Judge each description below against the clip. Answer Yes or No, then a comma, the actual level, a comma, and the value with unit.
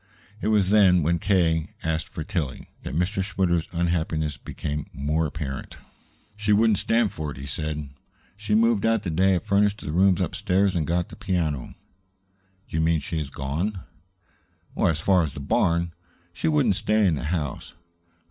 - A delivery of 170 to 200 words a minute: Yes, average, 175 wpm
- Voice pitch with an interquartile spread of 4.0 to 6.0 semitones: Yes, average, 4.3 semitones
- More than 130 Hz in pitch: No, very low, 85 Hz